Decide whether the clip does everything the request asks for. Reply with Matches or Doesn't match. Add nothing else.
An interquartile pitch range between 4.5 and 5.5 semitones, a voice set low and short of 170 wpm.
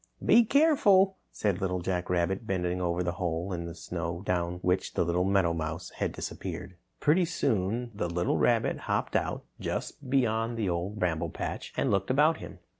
Doesn't match